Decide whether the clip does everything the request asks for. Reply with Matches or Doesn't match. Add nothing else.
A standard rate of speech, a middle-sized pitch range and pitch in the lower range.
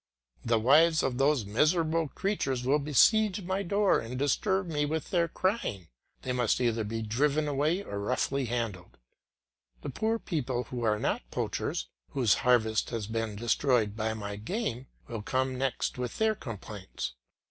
Doesn't match